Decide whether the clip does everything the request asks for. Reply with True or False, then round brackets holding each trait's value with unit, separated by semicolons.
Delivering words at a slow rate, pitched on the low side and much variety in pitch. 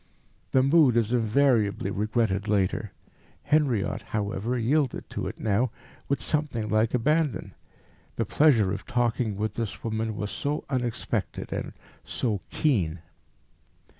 False (125 wpm; 115 Hz; 3.9 semitones)